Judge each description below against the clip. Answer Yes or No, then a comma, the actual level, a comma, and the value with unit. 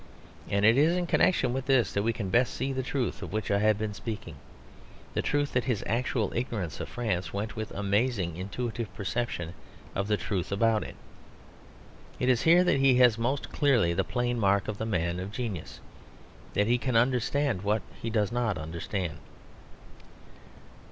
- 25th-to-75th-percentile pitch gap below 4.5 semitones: Yes, average, 3.8 semitones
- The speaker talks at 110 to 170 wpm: No, average, 180 wpm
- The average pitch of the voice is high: No, low, 110 Hz